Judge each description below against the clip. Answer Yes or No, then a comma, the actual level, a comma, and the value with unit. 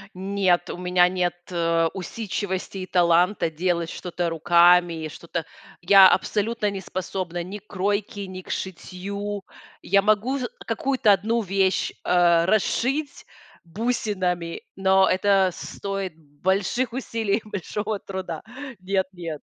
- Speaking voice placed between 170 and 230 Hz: Yes, high, 190 Hz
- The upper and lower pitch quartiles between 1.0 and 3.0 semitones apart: Yes, narrow, 2.6 semitones